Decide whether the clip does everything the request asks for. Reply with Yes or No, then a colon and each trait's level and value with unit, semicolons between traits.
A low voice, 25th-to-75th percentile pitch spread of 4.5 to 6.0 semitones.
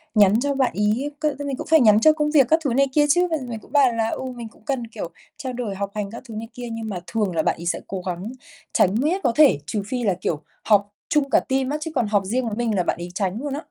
No: high, 230 Hz; average, 5.2 semitones